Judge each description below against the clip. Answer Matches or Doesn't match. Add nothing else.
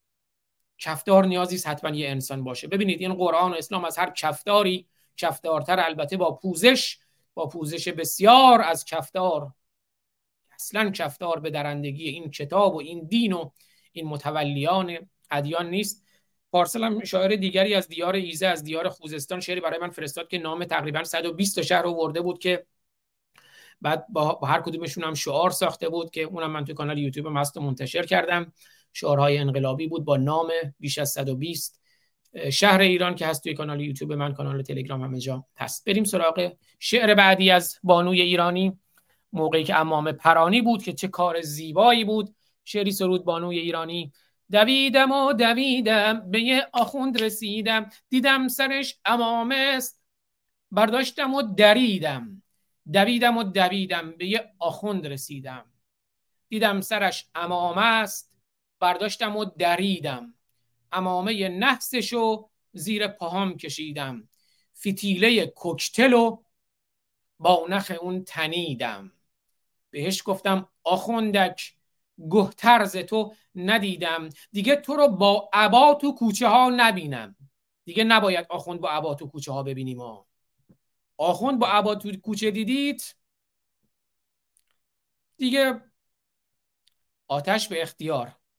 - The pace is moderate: Matches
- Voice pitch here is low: Doesn't match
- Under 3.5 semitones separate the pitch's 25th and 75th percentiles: Doesn't match